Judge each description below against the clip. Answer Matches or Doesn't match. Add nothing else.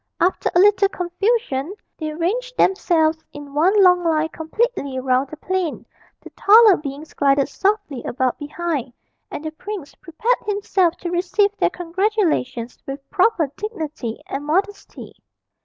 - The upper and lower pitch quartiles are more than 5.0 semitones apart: Matches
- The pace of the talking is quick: Doesn't match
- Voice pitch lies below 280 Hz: Doesn't match